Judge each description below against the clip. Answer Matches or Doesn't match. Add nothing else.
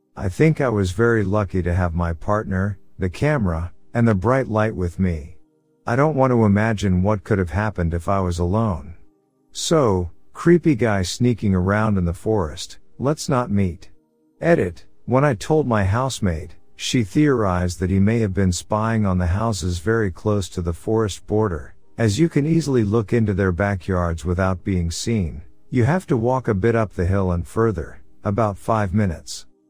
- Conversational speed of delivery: Matches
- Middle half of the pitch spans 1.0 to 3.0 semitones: Doesn't match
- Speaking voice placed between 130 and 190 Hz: Doesn't match